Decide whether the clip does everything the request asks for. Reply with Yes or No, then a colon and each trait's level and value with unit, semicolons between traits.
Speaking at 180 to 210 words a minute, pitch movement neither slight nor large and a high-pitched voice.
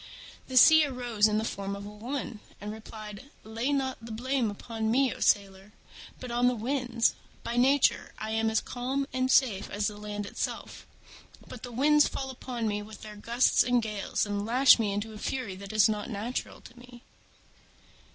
Yes: average, 190 wpm; average, 3.2 semitones; high, 225 Hz